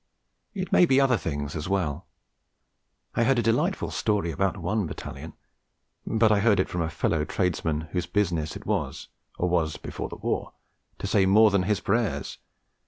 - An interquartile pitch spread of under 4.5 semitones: No, average, 4.9 semitones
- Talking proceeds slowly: No, average, 175 wpm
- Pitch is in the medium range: No, very low, 95 Hz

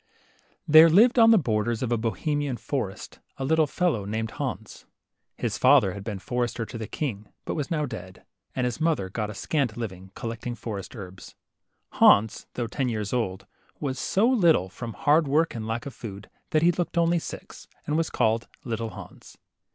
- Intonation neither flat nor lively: No, wide, 6.2 semitones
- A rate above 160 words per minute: Yes, average, 190 wpm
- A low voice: Yes, low, 120 Hz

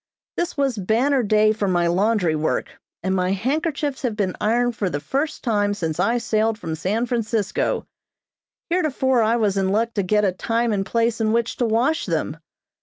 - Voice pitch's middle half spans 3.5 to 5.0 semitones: Yes, average, 3.8 semitones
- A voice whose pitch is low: No, high, 220 Hz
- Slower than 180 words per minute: No, average, 185 wpm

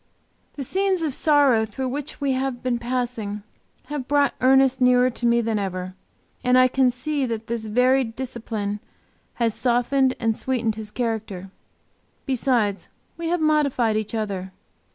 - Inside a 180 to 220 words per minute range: No, average, 155 wpm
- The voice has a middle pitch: No, very high, 250 Hz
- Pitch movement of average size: Yes, average, 3.3 semitones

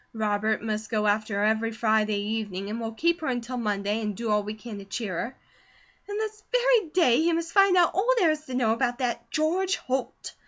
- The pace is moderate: No, fast, 225 wpm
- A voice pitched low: No, high, 230 Hz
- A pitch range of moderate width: No, wide, 7.4 semitones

